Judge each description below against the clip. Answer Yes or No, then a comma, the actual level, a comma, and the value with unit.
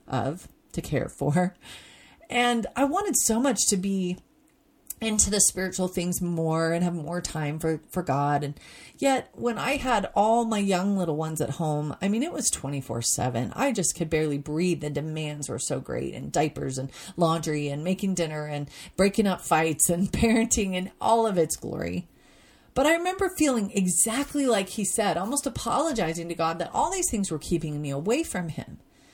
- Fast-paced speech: No, average, 185 wpm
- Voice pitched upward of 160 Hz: Yes, medium, 185 Hz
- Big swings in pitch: Yes, wide, 6.5 semitones